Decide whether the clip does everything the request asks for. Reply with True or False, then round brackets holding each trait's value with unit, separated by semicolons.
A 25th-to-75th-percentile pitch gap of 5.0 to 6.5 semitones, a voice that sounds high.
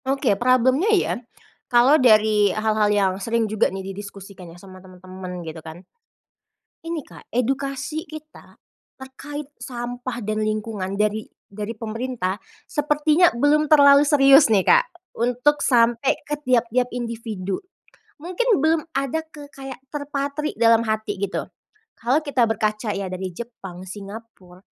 True (5.4 semitones; 235 Hz)